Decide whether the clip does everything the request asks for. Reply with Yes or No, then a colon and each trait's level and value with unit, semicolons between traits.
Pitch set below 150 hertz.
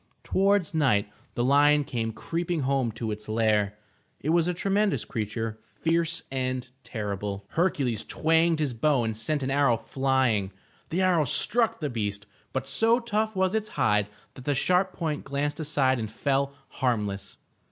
Yes: low, 135 Hz